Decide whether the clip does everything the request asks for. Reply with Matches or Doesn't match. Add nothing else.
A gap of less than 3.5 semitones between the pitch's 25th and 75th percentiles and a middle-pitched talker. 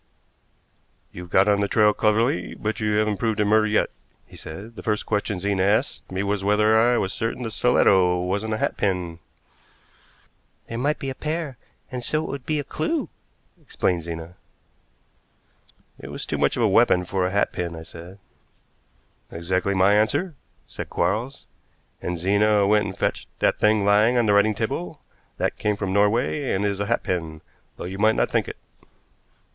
Doesn't match